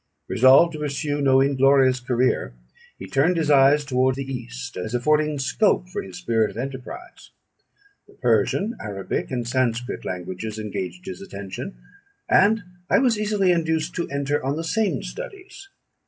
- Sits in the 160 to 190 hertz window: No, low, 135 Hz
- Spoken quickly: No, average, 155 wpm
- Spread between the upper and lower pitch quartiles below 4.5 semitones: No, average, 5.3 semitones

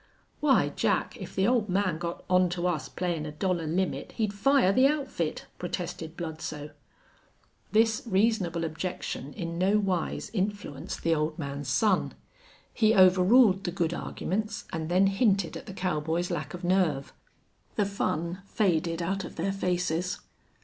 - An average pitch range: Yes, average, 3.2 semitones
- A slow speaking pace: No, average, 150 wpm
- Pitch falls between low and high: Yes, medium, 180 Hz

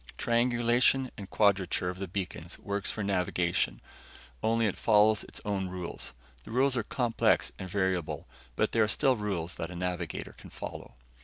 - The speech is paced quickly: No, average, 165 wpm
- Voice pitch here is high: No, low, 100 Hz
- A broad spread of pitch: No, average, 4.1 semitones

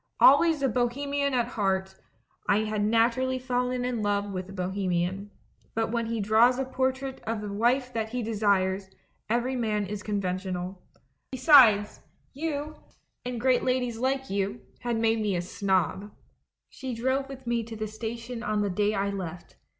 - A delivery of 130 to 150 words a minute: No, average, 170 wpm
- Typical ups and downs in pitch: Yes, average, 4.0 semitones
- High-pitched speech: Yes, high, 225 Hz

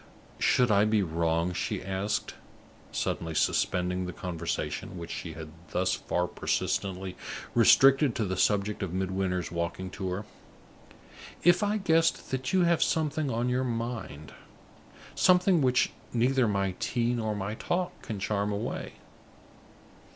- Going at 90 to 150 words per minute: Yes, slow, 135 wpm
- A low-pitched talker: Yes, low, 105 Hz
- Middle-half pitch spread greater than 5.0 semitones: Yes, wide, 5.6 semitones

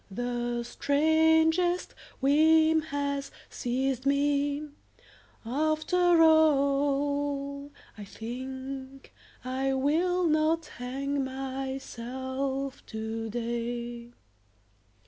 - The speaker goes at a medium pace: No, slow, 65 wpm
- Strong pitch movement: No, average, 3.2 semitones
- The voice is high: Yes, very high, 275 Hz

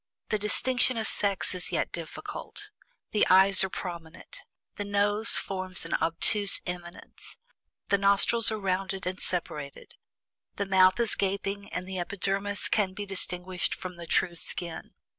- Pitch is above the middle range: Yes, high, 195 Hz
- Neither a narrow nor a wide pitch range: No, narrow, 2.0 semitones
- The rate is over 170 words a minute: No, average, 145 wpm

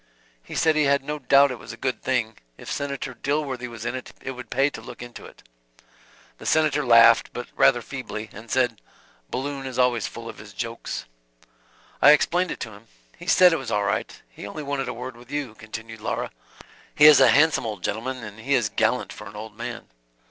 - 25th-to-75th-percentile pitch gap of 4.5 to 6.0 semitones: No, average, 3.7 semitones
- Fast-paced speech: Yes, fast, 215 wpm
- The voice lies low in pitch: Yes, low, 125 Hz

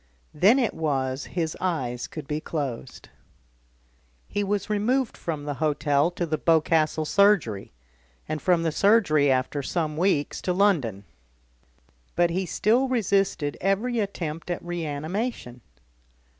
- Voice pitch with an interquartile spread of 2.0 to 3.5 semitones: No, average, 5.2 semitones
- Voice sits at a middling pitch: Yes, medium, 165 Hz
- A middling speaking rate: No, slow, 130 wpm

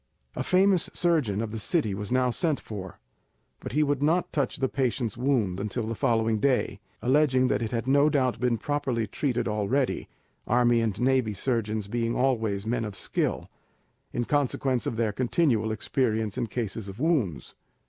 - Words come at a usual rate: Yes, average, 170 wpm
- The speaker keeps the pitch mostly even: No, average, 3.8 semitones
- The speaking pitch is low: Yes, low, 120 Hz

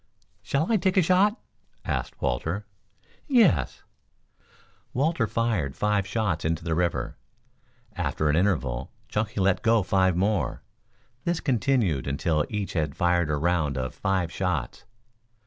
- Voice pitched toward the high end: No, very low, 95 Hz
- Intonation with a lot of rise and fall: Yes, wide, 6.4 semitones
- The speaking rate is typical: No, slow, 130 wpm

